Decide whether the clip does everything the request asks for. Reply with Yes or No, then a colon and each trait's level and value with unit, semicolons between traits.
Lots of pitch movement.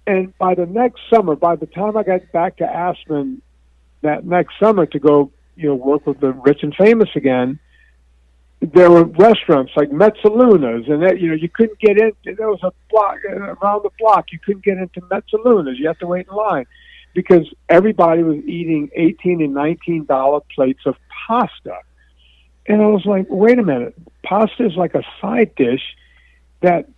Yes: wide, 6.0 semitones